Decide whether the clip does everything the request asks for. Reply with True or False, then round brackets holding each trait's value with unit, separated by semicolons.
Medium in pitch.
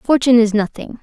False (235 Hz)